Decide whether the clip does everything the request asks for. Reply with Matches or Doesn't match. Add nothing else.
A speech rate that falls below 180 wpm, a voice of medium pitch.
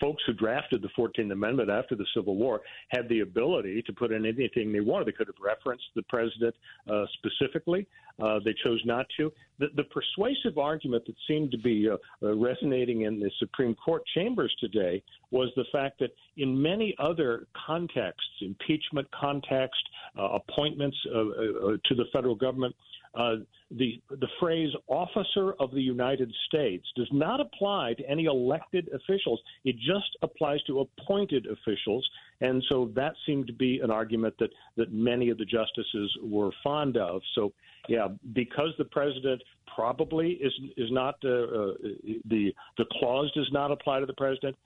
Doesn't match